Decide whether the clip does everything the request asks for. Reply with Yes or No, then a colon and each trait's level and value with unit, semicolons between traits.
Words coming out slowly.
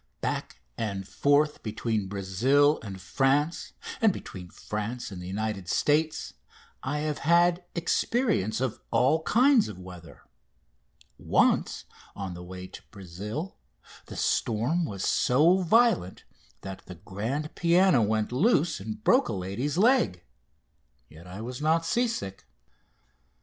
Yes: slow, 130 wpm